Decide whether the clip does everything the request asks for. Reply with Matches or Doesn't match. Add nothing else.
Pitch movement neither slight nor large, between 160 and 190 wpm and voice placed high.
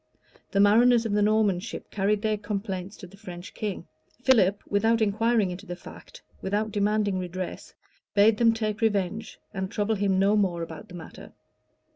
Doesn't match